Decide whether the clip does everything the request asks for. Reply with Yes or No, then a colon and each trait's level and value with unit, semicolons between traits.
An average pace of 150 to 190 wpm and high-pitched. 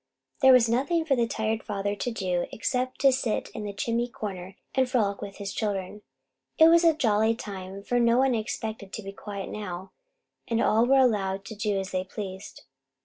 No: average, 200 wpm; high, 215 Hz